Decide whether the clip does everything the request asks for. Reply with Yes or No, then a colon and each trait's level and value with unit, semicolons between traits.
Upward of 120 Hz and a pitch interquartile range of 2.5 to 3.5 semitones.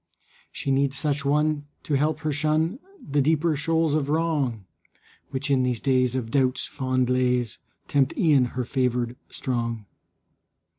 Yes: medium, 140 Hz; average, 3.0 semitones